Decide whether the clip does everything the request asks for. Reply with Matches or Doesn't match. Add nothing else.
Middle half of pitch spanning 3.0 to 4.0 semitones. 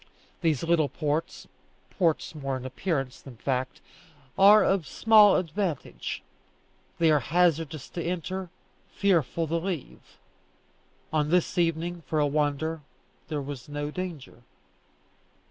Matches